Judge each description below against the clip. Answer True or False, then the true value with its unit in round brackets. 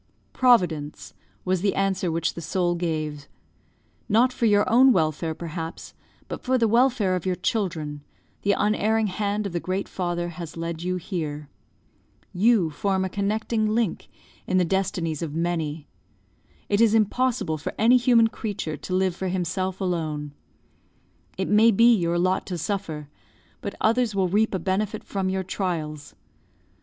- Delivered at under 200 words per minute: True (155 wpm)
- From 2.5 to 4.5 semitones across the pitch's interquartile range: True (4.1 semitones)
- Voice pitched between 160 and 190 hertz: True (185 Hz)